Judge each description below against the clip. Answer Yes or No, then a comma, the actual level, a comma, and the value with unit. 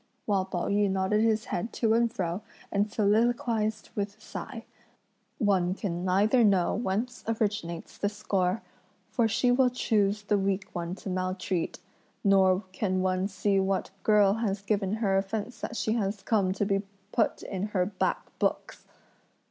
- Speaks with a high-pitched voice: Yes, high, 200 Hz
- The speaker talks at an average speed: Yes, average, 160 wpm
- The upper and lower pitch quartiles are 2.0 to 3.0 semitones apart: Yes, narrow, 2.4 semitones